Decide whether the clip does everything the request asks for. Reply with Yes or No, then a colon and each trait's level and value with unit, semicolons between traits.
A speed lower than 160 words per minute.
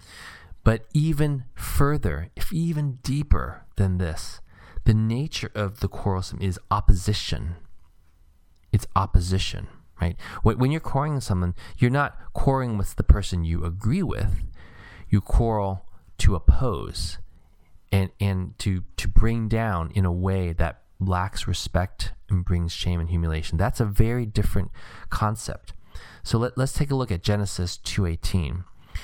Yes: average, 140 wpm